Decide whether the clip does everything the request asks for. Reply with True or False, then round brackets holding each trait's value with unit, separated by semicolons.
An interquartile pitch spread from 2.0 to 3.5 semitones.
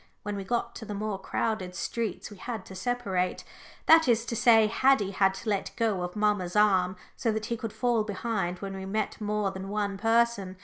True (3.0 semitones)